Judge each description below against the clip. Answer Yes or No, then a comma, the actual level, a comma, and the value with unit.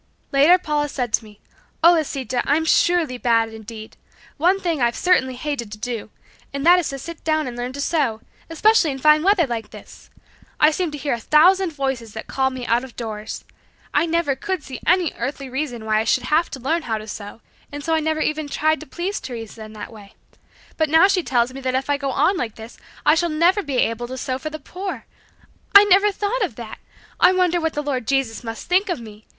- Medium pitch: No, very high, 280 Hz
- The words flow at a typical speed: No, fast, 230 wpm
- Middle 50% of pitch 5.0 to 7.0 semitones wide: Yes, wide, 5.6 semitones